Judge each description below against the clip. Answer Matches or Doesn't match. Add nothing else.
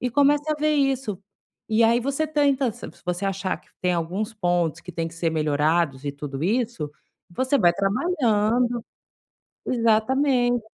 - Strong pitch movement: Matches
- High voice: Matches